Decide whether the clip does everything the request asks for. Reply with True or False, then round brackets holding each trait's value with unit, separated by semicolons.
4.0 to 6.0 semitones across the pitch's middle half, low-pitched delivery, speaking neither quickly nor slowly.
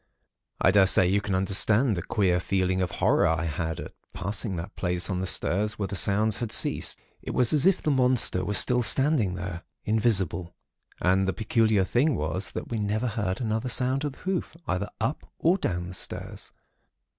True (4.3 semitones; 100 Hz; 190 wpm)